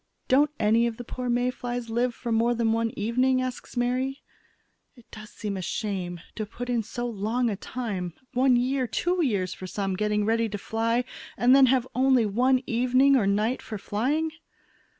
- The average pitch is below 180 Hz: No, high, 235 Hz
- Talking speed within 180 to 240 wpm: Yes, average, 190 wpm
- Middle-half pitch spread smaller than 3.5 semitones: Yes, average, 2.9 semitones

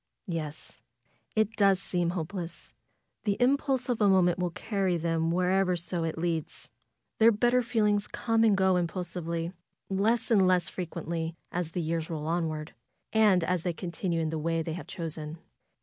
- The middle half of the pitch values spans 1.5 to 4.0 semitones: Yes, average, 3.5 semitones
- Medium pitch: Yes, medium, 180 Hz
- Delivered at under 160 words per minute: No, average, 180 wpm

